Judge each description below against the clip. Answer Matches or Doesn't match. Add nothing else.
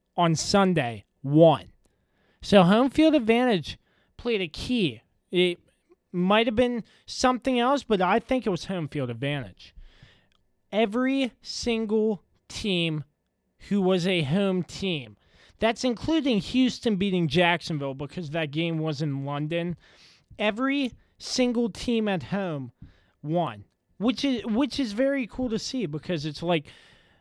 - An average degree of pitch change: Doesn't match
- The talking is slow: Matches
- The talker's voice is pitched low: Doesn't match